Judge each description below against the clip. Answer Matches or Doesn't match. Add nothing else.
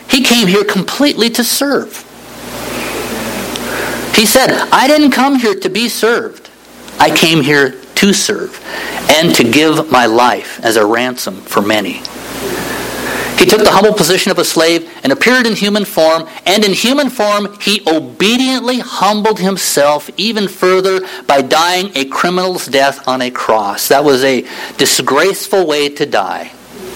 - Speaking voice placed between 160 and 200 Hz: Matches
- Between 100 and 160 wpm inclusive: Matches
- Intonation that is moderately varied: Doesn't match